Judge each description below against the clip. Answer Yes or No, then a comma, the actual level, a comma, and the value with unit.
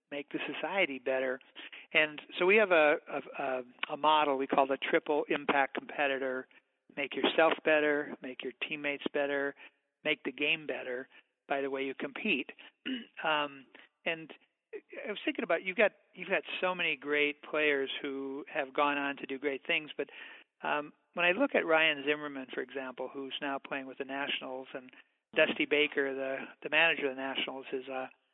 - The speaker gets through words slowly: No, average, 175 wpm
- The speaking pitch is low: No, medium, 145 Hz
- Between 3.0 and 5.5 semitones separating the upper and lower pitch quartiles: No, narrow, 2.5 semitones